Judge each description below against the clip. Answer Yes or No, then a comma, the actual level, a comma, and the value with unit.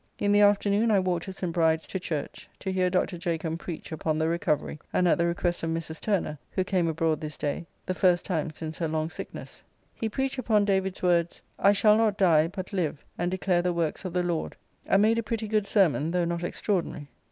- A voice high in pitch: No, medium, 175 Hz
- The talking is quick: Yes, fast, 220 wpm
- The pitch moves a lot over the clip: No, average, 3.3 semitones